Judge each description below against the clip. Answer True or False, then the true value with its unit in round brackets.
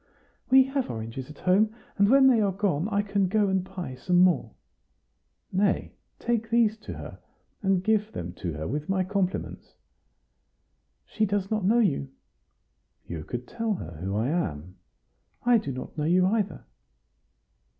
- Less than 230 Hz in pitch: True (190 Hz)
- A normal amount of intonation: False (6.9 semitones)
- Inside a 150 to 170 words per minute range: True (160 wpm)